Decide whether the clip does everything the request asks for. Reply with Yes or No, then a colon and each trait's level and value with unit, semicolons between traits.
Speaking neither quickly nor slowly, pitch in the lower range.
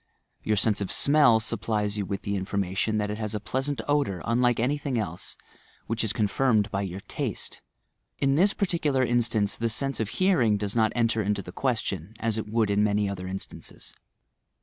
Yes: average, 185 wpm; low, 110 Hz